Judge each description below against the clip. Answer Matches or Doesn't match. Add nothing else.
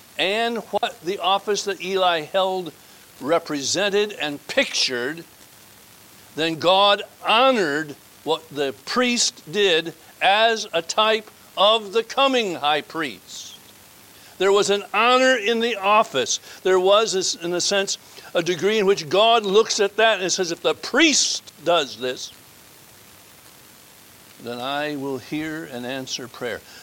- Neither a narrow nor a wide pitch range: Doesn't match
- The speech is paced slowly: Matches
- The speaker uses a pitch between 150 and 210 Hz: Matches